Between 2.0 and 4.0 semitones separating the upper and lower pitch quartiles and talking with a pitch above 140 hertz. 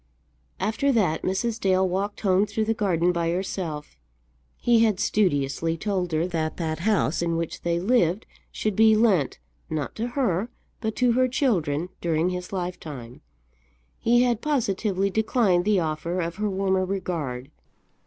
No: average, 4.5 semitones; medium, 185 Hz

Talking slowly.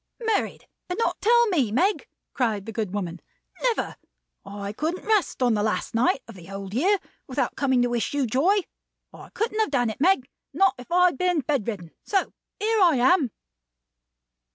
No: average, 185 wpm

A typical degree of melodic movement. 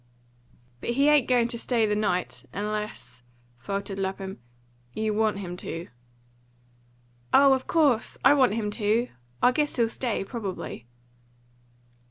Yes: average, 4.0 semitones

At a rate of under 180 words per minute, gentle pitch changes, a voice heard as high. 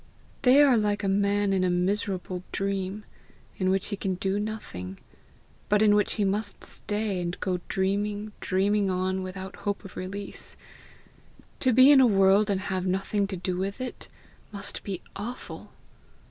Yes: average, 165 wpm; narrow, 1.7 semitones; high, 200 Hz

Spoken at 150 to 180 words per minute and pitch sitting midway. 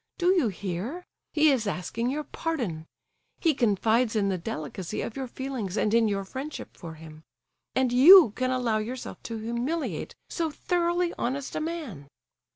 No: average, 160 wpm; high, 245 Hz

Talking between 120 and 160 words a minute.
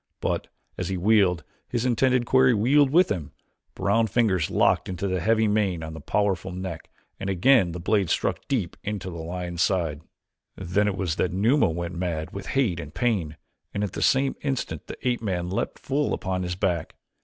No: average, 190 wpm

